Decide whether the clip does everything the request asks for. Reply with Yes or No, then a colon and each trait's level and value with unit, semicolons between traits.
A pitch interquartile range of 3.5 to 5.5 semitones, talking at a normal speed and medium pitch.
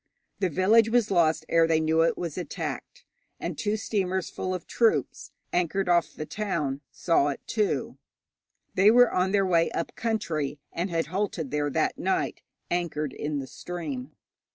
Yes: average, 4.0 semitones; average, 165 wpm; medium, 175 Hz